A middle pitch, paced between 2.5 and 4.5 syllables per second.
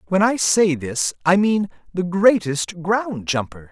Yes: medium, 175 Hz; 3.8 syllables/s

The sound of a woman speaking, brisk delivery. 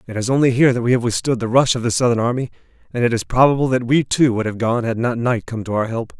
No: male; fast, 300 wpm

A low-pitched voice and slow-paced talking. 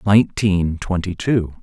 Yes: very low, 95 Hz; slow, 110 wpm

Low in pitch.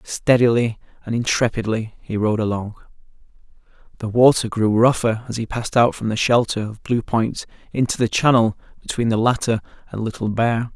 Yes: low, 115 Hz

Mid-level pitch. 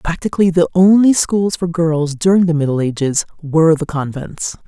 Yes: medium, 165 Hz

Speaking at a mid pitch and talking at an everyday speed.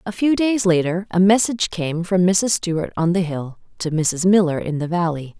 No: medium, 180 Hz; fast, 210 wpm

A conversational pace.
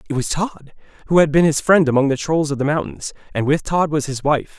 No: fast, 260 wpm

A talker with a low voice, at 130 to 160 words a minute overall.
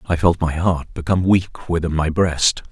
No: very low, 85 Hz; average, 200 wpm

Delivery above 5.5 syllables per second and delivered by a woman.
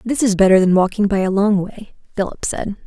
Yes: 5.7 syllables/s; female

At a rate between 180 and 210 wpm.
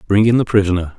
No: fast, 245 wpm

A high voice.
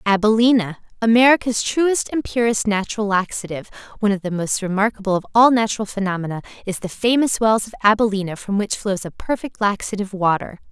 Yes: high, 210 Hz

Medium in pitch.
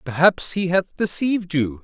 Yes: medium, 170 Hz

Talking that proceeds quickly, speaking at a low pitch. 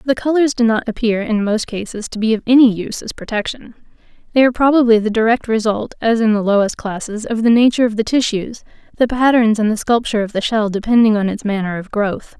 No: fast, 225 wpm; high, 225 Hz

